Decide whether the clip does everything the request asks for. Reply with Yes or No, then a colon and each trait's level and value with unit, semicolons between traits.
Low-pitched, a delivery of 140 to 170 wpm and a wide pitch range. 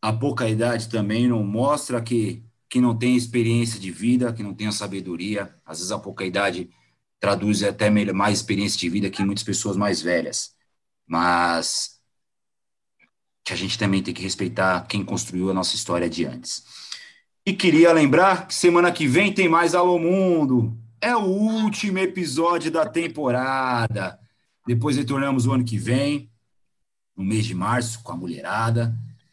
Yes: low, 115 Hz; average, 165 wpm; wide, 5.9 semitones